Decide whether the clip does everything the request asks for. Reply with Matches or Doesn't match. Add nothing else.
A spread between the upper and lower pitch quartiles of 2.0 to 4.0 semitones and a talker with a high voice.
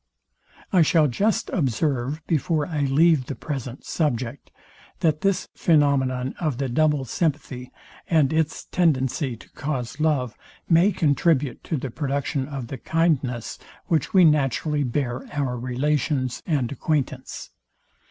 Doesn't match